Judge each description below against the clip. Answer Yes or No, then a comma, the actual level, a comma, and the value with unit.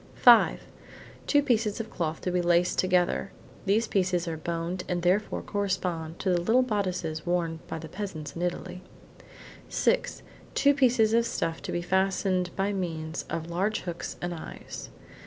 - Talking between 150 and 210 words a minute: Yes, average, 160 wpm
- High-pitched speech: No, medium, 180 Hz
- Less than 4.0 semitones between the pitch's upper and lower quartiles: Yes, average, 3.3 semitones